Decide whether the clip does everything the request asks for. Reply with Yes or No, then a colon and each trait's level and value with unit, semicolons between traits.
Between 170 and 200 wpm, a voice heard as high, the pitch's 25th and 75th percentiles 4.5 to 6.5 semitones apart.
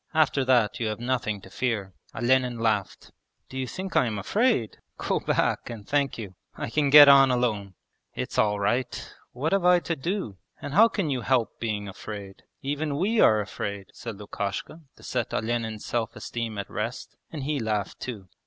No: average, 185 wpm; low, 120 Hz; average, 4.9 semitones